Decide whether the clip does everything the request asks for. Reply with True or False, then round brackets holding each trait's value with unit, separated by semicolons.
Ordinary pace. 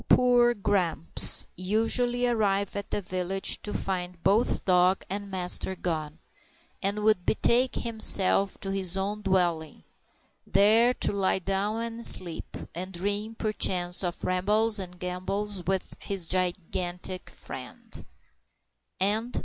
False (120 wpm)